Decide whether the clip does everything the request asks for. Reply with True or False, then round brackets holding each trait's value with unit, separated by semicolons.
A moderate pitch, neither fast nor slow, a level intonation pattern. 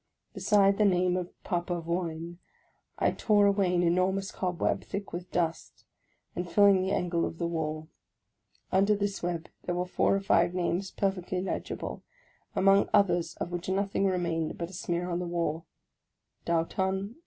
True (180 Hz; 165 wpm; 2.2 semitones)